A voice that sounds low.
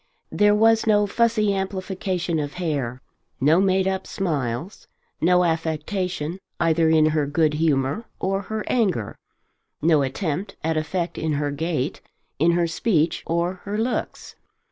No: medium, 170 Hz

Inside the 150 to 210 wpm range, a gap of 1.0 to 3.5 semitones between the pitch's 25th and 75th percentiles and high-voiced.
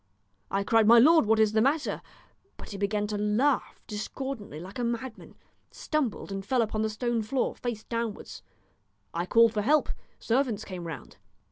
Yes: average, 170 wpm; average, 2.8 semitones; high, 220 Hz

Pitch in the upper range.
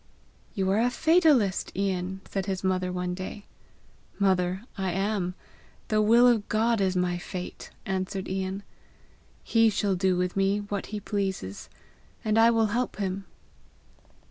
Yes: high, 195 Hz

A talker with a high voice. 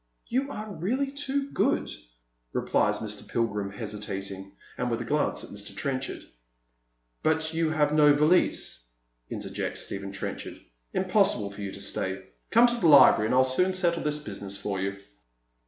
No: low, 130 Hz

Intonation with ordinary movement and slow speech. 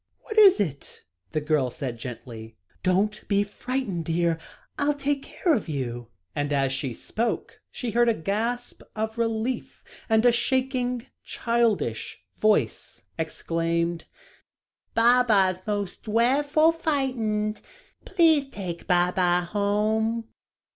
No: wide, 6.5 semitones; slow, 115 wpm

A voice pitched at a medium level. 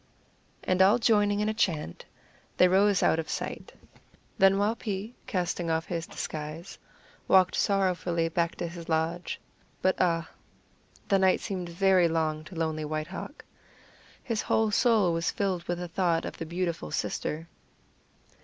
Yes: medium, 180 Hz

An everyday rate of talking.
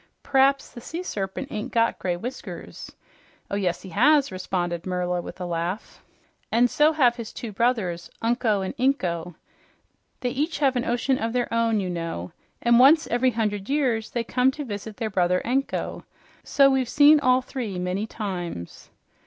Yes: average, 175 wpm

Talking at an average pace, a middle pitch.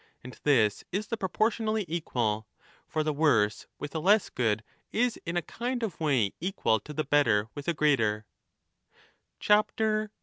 Yes: average, 155 wpm; medium, 150 Hz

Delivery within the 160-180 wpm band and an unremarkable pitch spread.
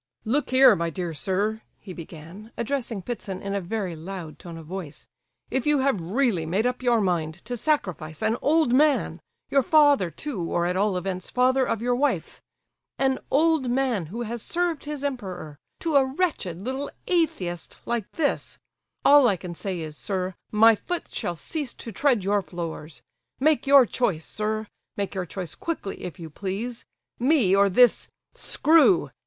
No: average, 165 wpm; wide, 6.8 semitones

